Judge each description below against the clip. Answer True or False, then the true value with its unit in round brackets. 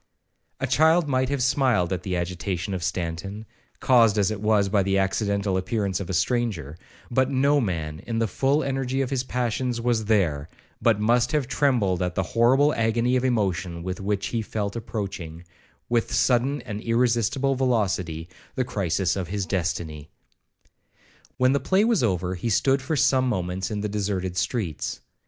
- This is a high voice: False (110 Hz)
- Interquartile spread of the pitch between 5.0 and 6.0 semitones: True (5.3 semitones)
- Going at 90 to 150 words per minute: False (170 wpm)